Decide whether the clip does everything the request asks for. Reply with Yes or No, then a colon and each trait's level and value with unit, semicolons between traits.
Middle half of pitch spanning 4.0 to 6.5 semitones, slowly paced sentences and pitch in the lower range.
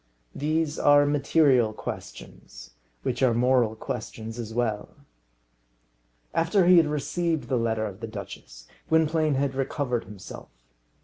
Yes: average, 5.3 semitones; slow, 125 wpm; low, 130 Hz